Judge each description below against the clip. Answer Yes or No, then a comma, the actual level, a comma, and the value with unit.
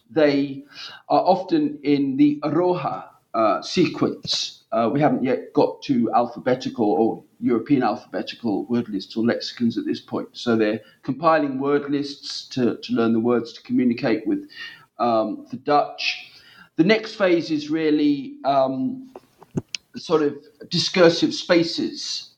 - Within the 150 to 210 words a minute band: No, slow, 135 wpm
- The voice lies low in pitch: No, medium, 170 Hz